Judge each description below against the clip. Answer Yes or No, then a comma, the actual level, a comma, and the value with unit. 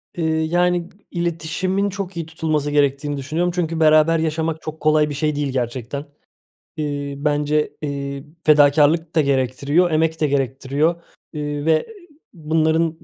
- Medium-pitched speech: Yes, medium, 155 Hz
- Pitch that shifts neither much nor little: No, narrow, 2.2 semitones